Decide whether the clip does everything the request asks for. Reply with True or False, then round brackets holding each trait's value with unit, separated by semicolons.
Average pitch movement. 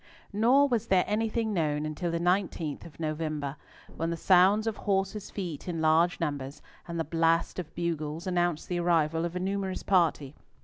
True (3.4 semitones)